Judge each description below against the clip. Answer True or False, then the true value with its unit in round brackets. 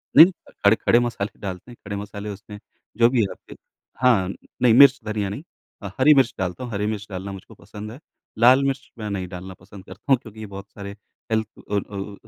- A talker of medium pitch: False (105 Hz)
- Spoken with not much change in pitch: False (3.3 semitones)